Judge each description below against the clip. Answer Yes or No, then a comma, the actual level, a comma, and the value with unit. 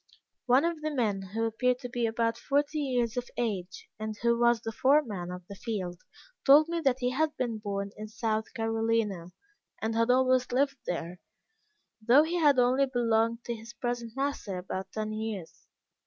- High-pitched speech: Yes, high, 230 Hz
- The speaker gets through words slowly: No, average, 180 wpm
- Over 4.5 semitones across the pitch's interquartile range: No, average, 3.1 semitones